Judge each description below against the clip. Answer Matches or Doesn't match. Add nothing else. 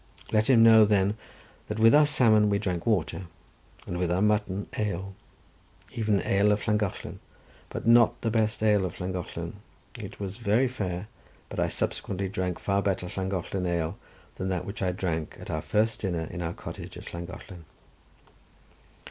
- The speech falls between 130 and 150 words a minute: Doesn't match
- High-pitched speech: Doesn't match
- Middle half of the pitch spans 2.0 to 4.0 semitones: Matches